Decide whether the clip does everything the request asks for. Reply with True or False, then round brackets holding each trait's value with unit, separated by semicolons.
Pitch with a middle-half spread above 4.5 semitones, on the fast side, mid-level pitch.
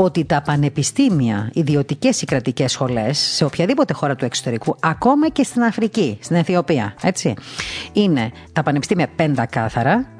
False (5.1 semitones; 140 wpm; 150 Hz)